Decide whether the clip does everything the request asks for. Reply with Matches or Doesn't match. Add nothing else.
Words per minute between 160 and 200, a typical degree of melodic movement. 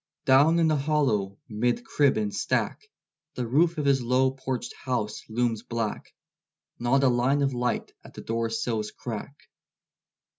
Doesn't match